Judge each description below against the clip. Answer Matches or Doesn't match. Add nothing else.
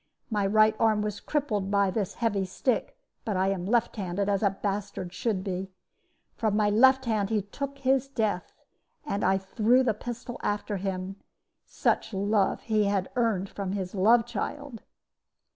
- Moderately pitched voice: Doesn't match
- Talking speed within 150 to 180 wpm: Matches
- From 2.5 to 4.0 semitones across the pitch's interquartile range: Matches